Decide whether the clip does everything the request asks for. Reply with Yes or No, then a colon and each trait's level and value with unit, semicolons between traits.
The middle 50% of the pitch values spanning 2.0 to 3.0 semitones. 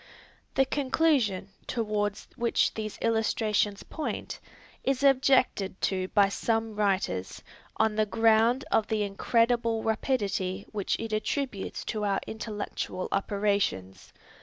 Yes: narrow, 2.5 semitones